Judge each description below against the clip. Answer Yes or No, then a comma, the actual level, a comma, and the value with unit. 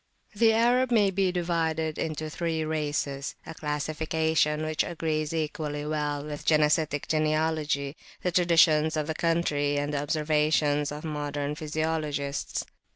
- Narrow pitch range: Yes, narrow, 1.6 semitones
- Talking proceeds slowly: Yes, slow, 125 wpm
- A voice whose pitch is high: No, medium, 155 Hz